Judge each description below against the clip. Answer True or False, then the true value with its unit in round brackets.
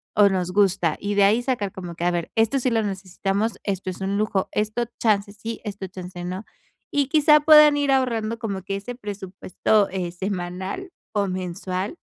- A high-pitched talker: True (200 Hz)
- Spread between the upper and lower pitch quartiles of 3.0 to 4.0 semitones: True (3.4 semitones)